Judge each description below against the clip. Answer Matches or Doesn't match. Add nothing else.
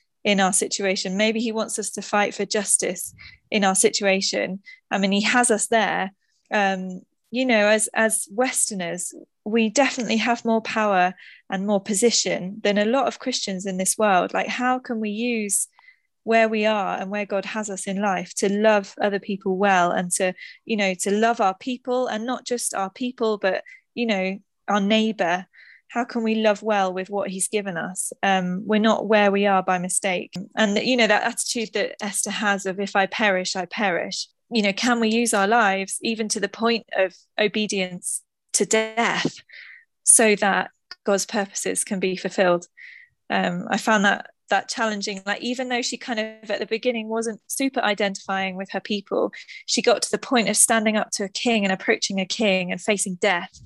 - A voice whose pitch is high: Matches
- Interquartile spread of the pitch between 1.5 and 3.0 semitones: Matches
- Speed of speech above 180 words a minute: Matches